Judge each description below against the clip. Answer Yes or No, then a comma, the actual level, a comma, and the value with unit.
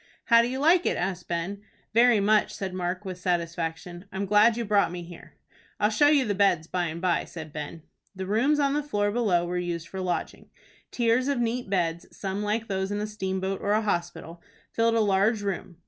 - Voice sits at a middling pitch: No, high, 195 Hz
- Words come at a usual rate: No, fast, 210 wpm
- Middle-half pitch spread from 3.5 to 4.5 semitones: Yes, average, 4.2 semitones